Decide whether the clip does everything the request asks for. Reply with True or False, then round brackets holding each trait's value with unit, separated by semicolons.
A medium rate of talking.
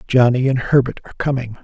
True (185 wpm)